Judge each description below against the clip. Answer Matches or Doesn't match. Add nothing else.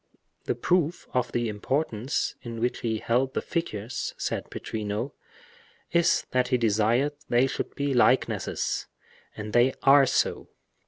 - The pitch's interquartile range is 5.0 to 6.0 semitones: Doesn't match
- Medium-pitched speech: Doesn't match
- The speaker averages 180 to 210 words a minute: Doesn't match